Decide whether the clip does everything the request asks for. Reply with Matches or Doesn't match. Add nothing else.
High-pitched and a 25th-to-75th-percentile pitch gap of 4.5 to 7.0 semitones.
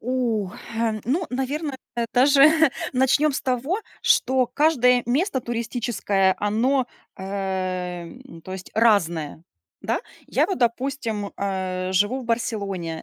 Matches